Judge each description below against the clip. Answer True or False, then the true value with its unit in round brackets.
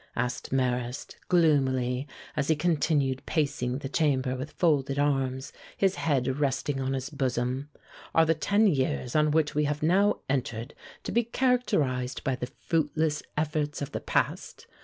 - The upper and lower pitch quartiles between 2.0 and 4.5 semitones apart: True (3.0 semitones)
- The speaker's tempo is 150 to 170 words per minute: True (155 wpm)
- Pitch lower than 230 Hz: True (140 Hz)